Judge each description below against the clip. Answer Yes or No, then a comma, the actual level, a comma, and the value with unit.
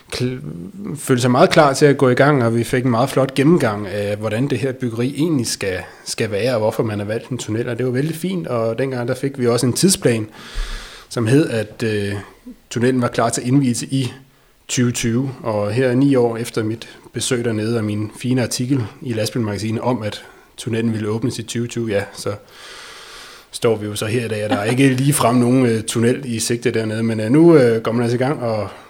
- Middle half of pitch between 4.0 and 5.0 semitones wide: No, average, 2.8 semitones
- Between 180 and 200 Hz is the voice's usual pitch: No, low, 120 Hz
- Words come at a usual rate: No, fast, 230 wpm